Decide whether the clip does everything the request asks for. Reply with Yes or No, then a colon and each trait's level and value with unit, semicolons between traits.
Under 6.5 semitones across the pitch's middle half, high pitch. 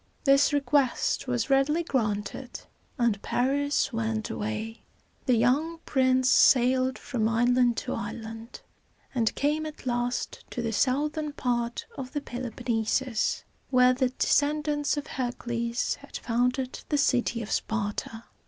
Yes: average, 2.9 semitones; very high, 250 Hz